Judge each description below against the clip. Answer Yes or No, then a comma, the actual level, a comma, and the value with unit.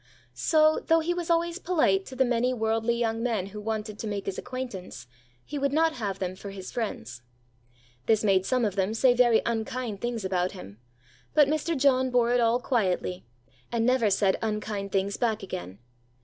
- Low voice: No, high, 225 Hz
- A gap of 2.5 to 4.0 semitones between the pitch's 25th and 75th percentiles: No, average, 4.4 semitones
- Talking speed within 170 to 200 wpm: Yes, average, 190 wpm